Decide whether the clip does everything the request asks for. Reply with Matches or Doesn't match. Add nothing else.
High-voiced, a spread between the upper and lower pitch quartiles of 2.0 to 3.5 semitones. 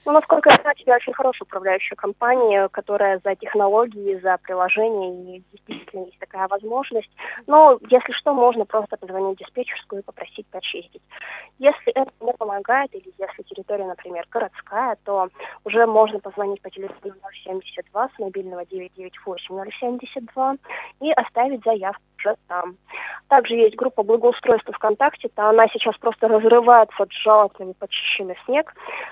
Doesn't match